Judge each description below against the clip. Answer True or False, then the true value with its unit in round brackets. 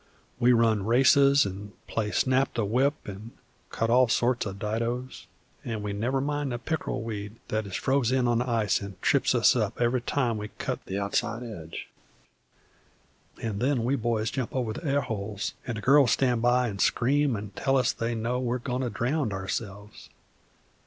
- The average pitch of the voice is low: True (120 Hz)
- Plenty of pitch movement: False (3.2 semitones)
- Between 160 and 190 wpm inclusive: True (185 wpm)